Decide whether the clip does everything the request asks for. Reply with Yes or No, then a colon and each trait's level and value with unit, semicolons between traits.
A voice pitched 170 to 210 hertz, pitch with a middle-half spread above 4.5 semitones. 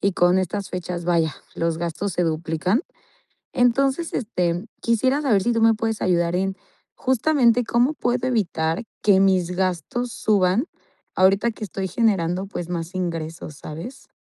Yes: high, 190 Hz; average, 5.2 semitones